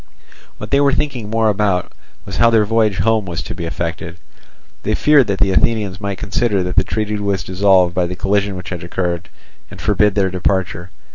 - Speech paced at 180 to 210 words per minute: Yes, average, 200 wpm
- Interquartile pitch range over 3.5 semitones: No, average, 2.9 semitones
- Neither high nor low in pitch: No, low, 100 Hz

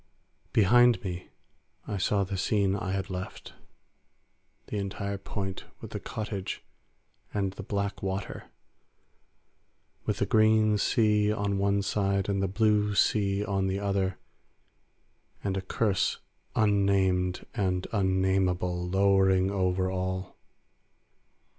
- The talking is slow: Yes, slow, 115 wpm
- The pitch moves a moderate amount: No, narrow, 1.4 semitones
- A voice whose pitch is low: Yes, low, 100 Hz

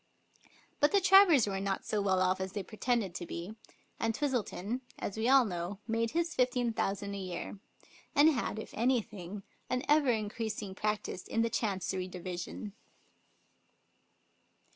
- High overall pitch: Yes, high, 215 Hz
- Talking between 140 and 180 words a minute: Yes, average, 150 wpm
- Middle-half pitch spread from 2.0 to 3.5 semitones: No, average, 4.6 semitones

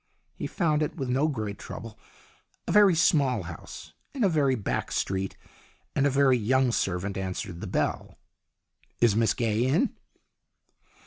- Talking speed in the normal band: Yes, average, 150 wpm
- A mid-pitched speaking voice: No, low, 125 Hz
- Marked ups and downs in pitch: Yes, wide, 6.0 semitones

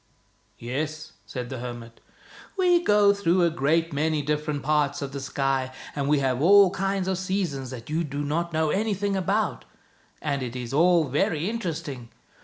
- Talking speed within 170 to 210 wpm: Yes, average, 180 wpm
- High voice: No, medium, 155 Hz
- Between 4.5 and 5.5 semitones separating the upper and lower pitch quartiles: Yes, average, 5.2 semitones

